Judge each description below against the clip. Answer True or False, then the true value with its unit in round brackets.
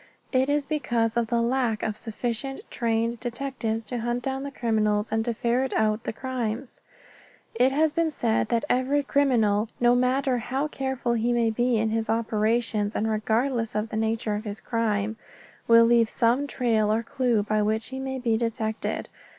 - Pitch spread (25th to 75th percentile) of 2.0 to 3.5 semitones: True (2.7 semitones)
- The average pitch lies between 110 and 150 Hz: False (235 Hz)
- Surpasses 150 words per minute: True (180 wpm)